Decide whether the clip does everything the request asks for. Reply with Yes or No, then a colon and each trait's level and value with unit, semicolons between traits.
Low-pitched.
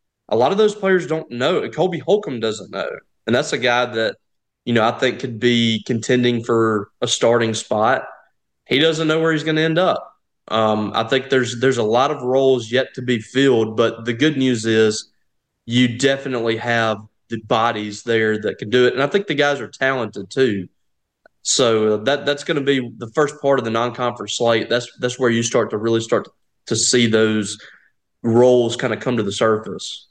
Yes: low, 120 Hz